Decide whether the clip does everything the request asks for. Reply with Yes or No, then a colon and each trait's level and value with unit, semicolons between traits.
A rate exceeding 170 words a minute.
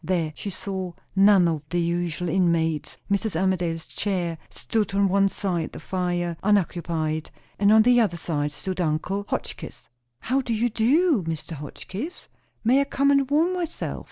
No: average, 165 wpm